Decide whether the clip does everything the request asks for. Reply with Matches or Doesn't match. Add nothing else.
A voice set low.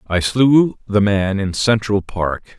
Matches